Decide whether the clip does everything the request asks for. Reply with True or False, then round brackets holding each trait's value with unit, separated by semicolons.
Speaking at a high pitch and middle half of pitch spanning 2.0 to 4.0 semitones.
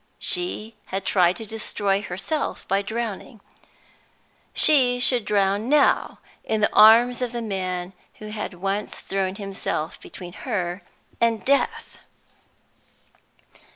True (210 Hz; 3.5 semitones)